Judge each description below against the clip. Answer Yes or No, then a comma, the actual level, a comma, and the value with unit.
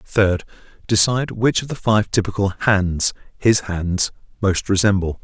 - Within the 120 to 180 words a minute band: Yes, average, 140 wpm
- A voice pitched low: Yes, low, 100 Hz